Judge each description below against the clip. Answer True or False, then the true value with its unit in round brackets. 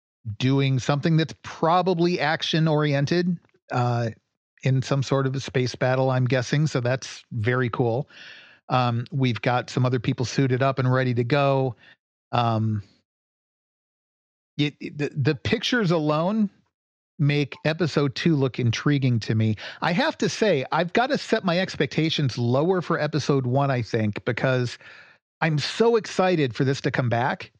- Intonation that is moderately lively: True (4.2 semitones)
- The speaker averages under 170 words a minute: True (155 wpm)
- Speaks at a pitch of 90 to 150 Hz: True (135 Hz)